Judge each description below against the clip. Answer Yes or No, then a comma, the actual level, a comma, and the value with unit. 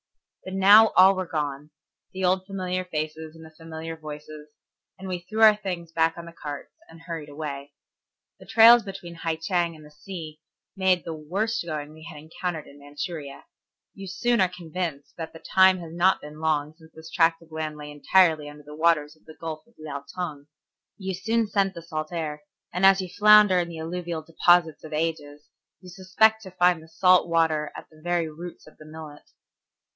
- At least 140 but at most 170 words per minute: No, average, 195 wpm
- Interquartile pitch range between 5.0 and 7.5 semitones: No, average, 3.0 semitones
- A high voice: No, medium, 165 Hz